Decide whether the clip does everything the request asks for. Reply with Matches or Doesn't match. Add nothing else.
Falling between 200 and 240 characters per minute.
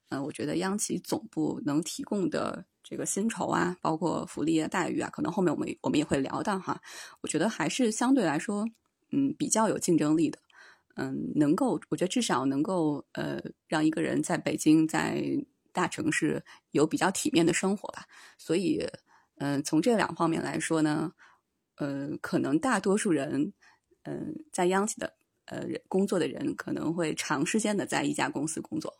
Doesn't match